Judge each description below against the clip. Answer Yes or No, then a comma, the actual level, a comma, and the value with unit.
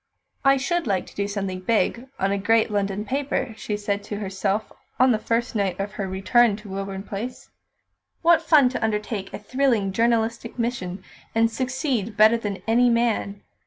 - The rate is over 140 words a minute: Yes, average, 175 wpm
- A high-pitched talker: Yes, high, 220 Hz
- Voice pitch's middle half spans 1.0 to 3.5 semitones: Yes, average, 3.2 semitones